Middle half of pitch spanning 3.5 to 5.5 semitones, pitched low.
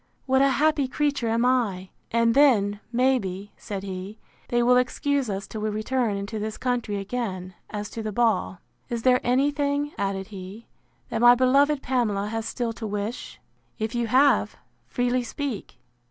No: average, 3.9 semitones; high, 235 Hz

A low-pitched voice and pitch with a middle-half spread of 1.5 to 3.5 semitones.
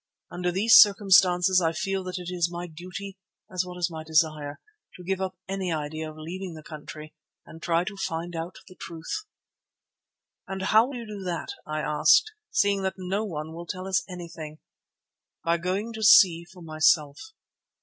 No: medium, 180 Hz; average, 2.9 semitones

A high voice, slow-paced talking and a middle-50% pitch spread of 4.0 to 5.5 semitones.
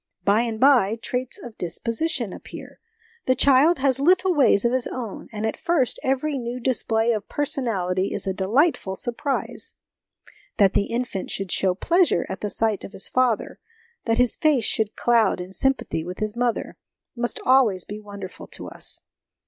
No: high, 235 Hz; average, 175 wpm; average, 4.5 semitones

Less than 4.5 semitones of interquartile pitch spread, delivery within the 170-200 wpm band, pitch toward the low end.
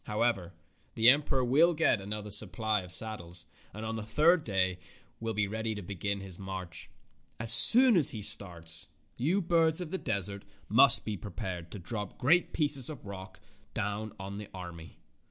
No: average, 5.0 semitones; average, 175 wpm; low, 105 Hz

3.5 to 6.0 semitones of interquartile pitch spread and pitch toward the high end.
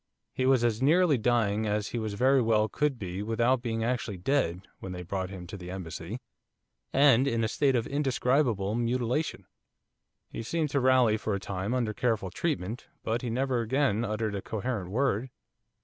No: average, 4.2 semitones; low, 115 Hz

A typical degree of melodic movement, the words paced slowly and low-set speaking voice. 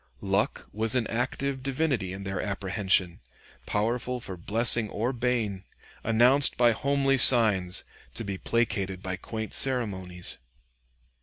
Yes: average, 4.4 semitones; slow, 125 wpm; low, 110 Hz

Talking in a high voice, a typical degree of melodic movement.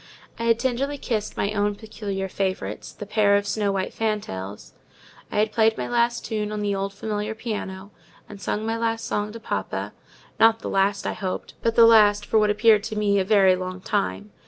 No: high, 210 Hz; narrow, 2.2 semitones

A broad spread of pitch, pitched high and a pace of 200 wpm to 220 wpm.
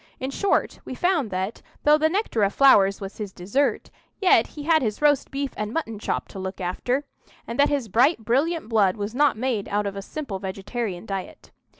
Yes: wide, 6.4 semitones; high, 230 Hz; fast, 205 wpm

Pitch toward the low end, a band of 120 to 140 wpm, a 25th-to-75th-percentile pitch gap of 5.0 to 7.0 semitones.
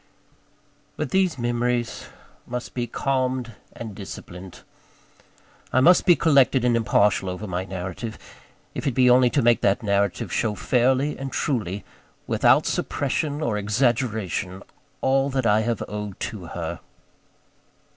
No: low, 120 Hz; slow, 135 wpm; average, 4.2 semitones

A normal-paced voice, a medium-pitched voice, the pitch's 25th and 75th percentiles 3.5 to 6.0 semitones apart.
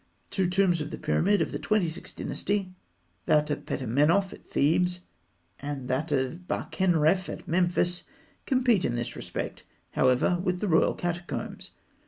Yes: average, 150 wpm; medium, 175 Hz; average, 3.8 semitones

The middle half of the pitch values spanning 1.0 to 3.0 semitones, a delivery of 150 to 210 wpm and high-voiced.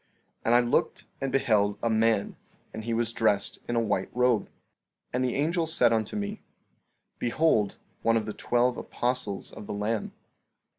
No: average, 2.7 semitones; average, 180 wpm; low, 115 Hz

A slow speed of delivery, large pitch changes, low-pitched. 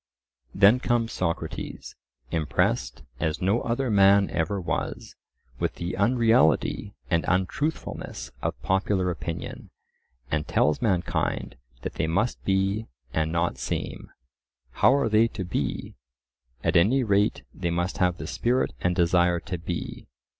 No: slow, 130 wpm; average, 4.1 semitones; very low, 95 Hz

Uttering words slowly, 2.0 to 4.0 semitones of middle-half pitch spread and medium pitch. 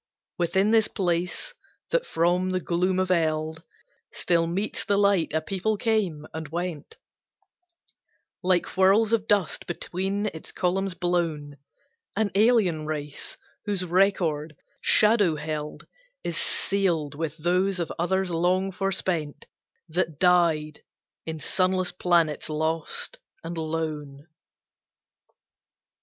Yes: slow, 115 wpm; average, 3.3 semitones; medium, 175 Hz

